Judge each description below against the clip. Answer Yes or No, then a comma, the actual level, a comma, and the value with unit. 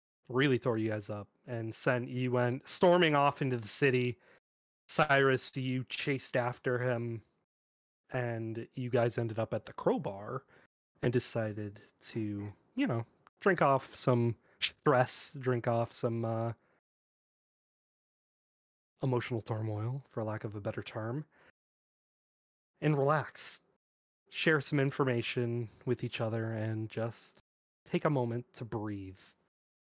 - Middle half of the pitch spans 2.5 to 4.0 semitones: Yes, average, 2.9 semitones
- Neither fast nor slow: No, slow, 125 wpm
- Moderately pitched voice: No, low, 120 Hz